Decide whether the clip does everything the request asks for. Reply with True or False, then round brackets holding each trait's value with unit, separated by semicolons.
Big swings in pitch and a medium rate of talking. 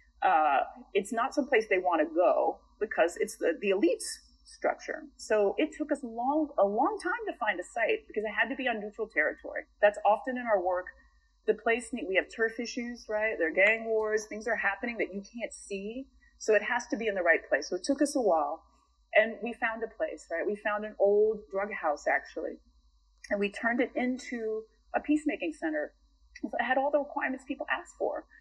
False (5.8 semitones; 215 wpm)